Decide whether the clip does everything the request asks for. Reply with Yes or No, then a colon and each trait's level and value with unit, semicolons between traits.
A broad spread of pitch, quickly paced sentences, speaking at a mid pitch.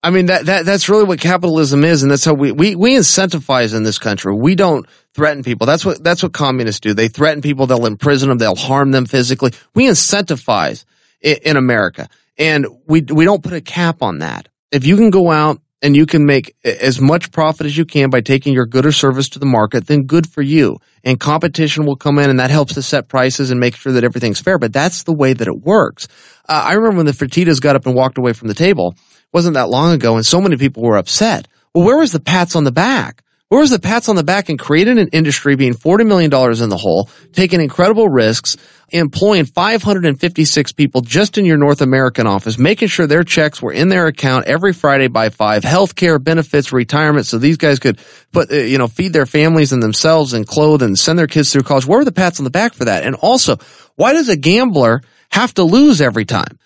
No: average, 4.7 semitones; fast, 235 wpm; medium, 150 Hz